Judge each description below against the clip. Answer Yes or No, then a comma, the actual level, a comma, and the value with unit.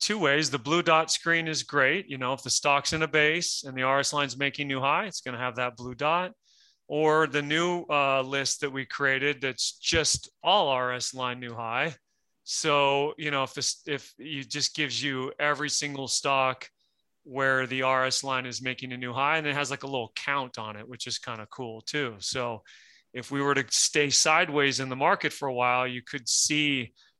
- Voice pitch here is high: No, medium, 140 Hz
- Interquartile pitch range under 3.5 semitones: Yes, narrow, 2.5 semitones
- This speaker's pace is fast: Yes, fast, 215 wpm